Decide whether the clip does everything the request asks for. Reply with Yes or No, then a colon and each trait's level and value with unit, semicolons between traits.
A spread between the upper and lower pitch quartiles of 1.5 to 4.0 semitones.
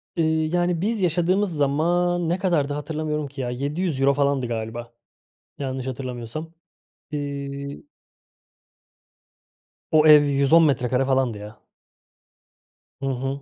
Yes: average, 3.6 semitones